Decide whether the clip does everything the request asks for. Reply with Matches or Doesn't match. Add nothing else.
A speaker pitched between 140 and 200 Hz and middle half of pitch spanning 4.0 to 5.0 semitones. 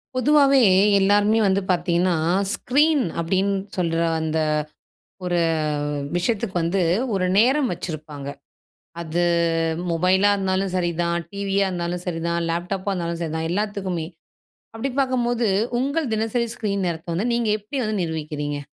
Matches